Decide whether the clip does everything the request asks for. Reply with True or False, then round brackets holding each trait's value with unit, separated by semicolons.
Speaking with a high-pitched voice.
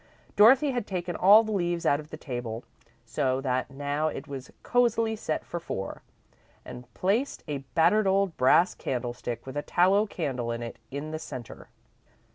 False (155 Hz)